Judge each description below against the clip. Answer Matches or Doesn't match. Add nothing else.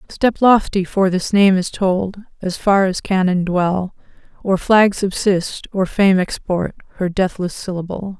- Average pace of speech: Matches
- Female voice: Matches